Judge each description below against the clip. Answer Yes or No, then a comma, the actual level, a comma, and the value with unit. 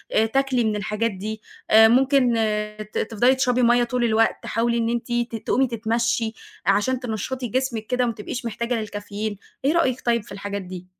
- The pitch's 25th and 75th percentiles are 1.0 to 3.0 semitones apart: Yes, narrow, 2.5 semitones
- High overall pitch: Yes, high, 230 Hz